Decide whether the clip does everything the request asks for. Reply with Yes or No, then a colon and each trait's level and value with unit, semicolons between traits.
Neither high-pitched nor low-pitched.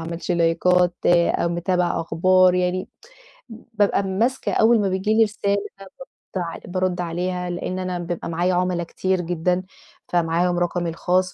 Yes: medium, 180 Hz